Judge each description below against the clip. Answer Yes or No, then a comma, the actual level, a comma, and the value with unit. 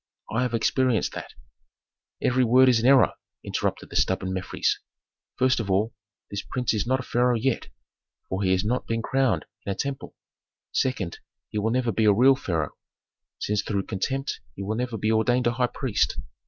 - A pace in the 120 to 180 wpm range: No, average, 190 wpm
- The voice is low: Yes, low, 115 Hz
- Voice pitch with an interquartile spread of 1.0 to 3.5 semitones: No, average, 3.9 semitones